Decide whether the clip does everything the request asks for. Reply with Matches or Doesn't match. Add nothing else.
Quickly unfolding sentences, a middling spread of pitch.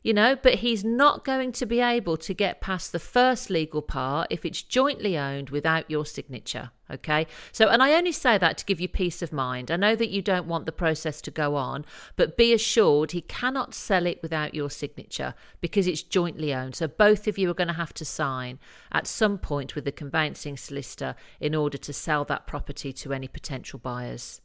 Doesn't match